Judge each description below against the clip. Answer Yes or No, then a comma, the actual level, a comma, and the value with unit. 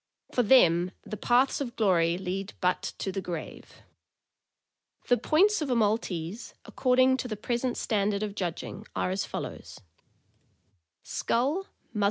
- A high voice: Yes, high, 215 Hz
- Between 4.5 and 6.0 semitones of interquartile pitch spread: Yes, average, 5.2 semitones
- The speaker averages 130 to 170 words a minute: Yes, average, 140 wpm